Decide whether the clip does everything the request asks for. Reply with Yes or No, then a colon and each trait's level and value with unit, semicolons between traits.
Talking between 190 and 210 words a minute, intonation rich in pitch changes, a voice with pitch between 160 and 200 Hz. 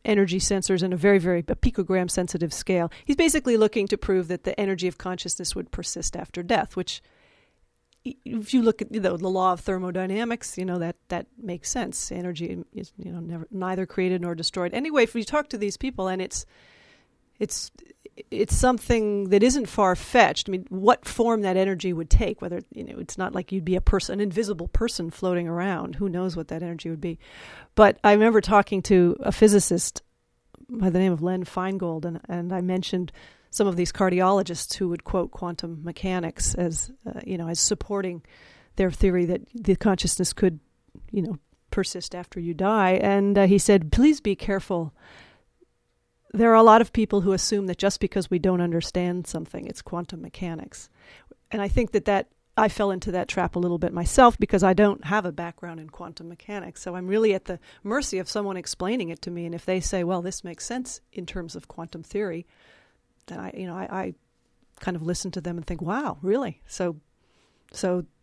No: average, 200 wpm; average, 2.8 semitones; medium, 185 Hz